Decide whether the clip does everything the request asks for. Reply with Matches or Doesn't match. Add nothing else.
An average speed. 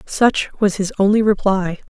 Matches